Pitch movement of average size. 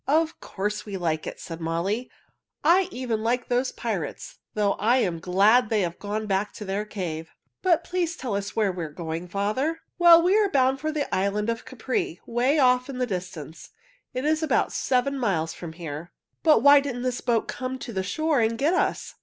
No: wide, 6.6 semitones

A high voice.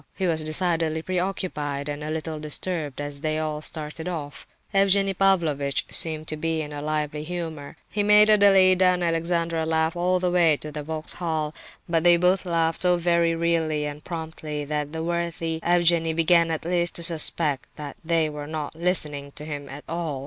No: medium, 160 Hz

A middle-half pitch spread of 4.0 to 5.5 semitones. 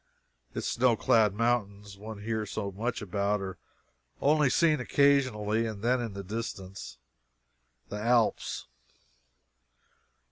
No: average, 3.1 semitones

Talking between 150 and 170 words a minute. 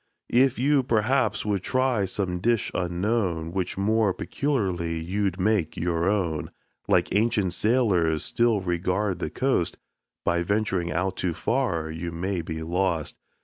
No: average, 140 wpm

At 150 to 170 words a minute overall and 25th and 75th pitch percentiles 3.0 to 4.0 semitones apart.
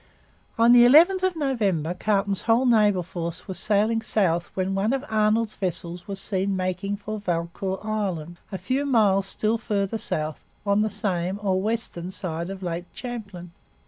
Yes: average, 165 wpm; average, 3.3 semitones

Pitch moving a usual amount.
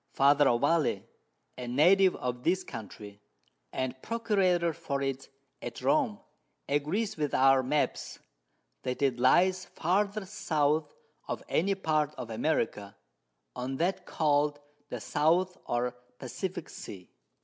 No: wide, 6.1 semitones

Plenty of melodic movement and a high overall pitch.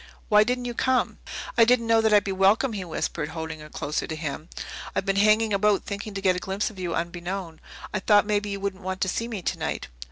No: average, 2.9 semitones; high, 200 Hz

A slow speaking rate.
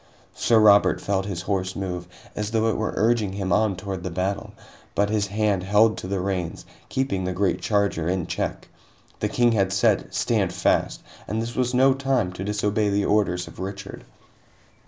No: average, 185 wpm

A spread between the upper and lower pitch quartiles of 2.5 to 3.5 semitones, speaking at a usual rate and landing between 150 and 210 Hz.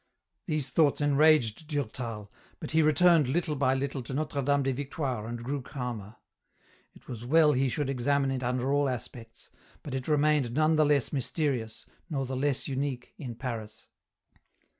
No: average, 3.1 semitones; average, 165 wpm; low, 135 Hz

